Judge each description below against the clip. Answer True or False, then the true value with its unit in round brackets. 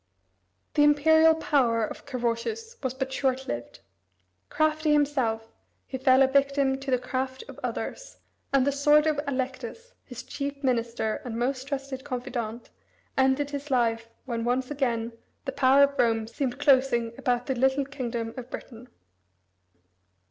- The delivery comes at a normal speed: True (150 wpm)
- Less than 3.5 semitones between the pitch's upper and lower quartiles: True (2.8 semitones)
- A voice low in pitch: False (265 Hz)